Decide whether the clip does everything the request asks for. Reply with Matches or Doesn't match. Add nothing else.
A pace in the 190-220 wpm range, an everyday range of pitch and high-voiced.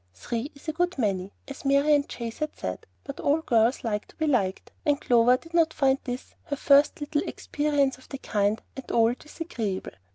Matches